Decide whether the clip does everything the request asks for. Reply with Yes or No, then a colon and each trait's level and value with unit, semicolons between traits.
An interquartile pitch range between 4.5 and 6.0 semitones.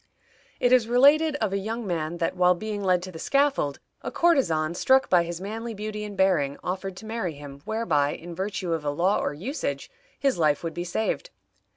Yes: average, 5.2 semitones